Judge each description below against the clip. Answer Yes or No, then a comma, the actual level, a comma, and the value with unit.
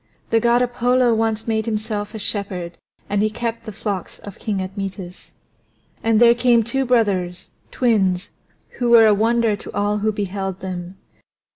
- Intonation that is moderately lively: Yes, average, 3.1 semitones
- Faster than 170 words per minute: No, average, 160 wpm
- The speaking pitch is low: No, high, 215 Hz